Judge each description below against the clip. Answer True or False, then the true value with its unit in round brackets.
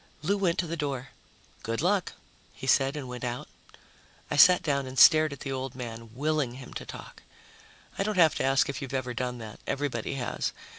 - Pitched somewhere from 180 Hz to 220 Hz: False (135 Hz)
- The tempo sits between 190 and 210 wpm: True (205 wpm)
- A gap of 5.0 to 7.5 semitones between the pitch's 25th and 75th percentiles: False (3.8 semitones)